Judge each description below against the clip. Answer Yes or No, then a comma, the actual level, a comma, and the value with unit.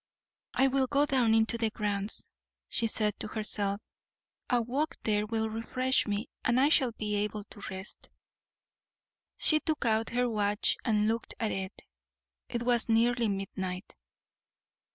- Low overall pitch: No, high, 225 Hz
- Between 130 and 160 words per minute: Yes, average, 150 wpm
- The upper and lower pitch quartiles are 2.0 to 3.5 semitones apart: Yes, average, 2.7 semitones